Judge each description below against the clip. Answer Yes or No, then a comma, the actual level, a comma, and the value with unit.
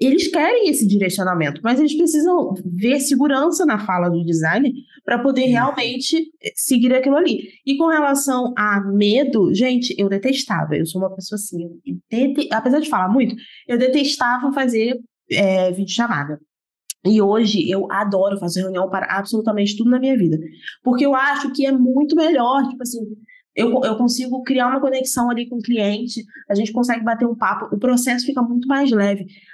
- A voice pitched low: No, high, 245 Hz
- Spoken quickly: No, average, 175 wpm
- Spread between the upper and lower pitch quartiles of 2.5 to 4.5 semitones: No, average, 5.2 semitones